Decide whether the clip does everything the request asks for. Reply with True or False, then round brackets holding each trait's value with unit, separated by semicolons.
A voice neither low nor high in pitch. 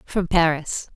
True (165 Hz)